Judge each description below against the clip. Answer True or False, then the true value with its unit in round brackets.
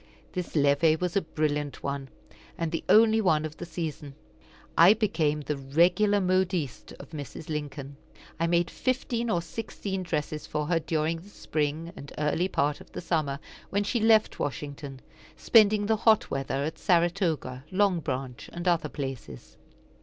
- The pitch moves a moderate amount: True (4.3 semitones)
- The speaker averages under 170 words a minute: True (160 wpm)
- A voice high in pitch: False (165 Hz)